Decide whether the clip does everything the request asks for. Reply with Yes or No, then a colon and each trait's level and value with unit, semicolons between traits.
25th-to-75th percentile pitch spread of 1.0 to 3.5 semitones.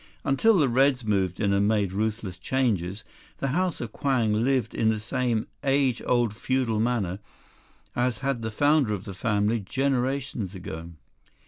No: average, 4.4 semitones